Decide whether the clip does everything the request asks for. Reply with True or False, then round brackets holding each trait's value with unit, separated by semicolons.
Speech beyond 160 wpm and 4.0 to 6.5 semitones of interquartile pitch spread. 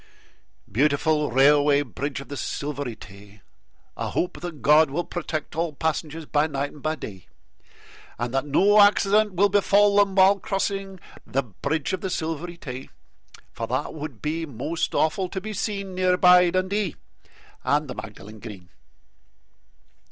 False (150 wpm; 5.1 semitones)